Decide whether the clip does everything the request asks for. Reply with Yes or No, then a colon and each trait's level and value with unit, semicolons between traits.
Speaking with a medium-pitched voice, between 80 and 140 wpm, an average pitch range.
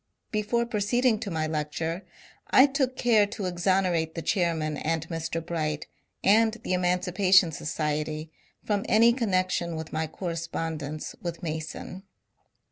Yes: medium, 175 Hz; slow, 135 wpm; average, 4.4 semitones